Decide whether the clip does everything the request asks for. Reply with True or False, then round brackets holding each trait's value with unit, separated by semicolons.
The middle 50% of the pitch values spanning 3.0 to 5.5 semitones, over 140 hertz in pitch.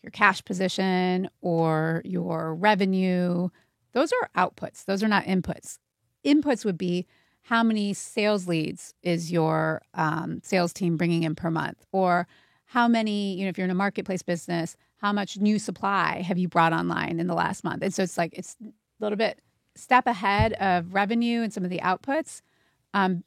True (3.4 semitones; 185 Hz)